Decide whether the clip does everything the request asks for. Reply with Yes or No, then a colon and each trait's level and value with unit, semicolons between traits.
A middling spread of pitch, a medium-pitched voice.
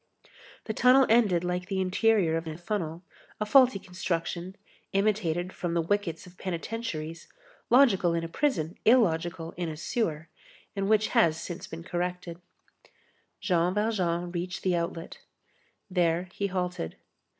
Yes: average, 3.3 semitones; medium, 180 Hz